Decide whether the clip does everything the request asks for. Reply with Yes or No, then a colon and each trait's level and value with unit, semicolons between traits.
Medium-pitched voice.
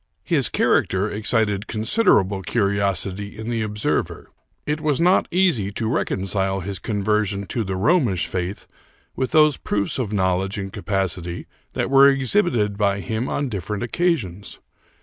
No: low, 105 Hz